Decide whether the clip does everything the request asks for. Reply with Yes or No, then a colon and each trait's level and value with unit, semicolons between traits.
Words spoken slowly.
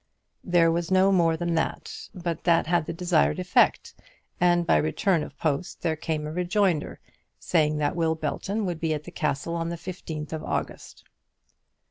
No: average, 175 wpm